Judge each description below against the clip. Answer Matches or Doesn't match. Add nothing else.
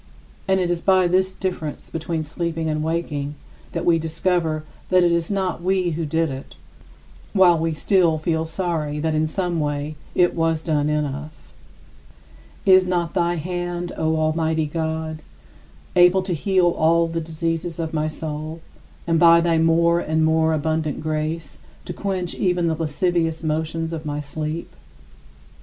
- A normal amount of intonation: Doesn't match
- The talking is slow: Doesn't match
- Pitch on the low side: Doesn't match